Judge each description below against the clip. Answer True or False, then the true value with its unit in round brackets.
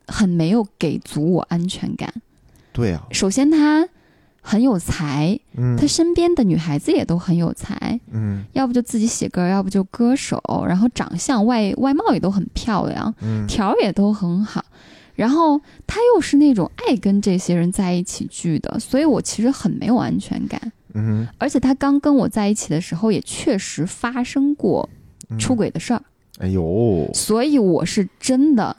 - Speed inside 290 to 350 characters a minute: False (250 characters per minute)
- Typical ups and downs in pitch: False (6.8 semitones)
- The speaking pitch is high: True (215 Hz)